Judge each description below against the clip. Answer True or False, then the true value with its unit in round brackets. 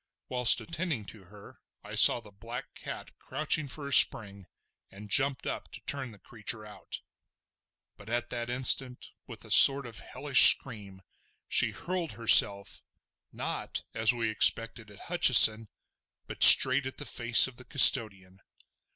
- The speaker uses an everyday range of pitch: True (4.1 semitones)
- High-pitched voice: False (120 Hz)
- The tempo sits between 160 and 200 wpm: False (150 wpm)